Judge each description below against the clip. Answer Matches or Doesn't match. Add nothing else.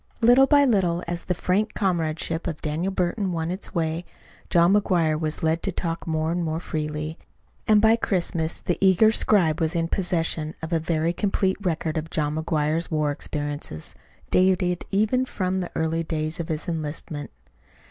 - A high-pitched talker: Doesn't match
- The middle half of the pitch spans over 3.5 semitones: Doesn't match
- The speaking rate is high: Doesn't match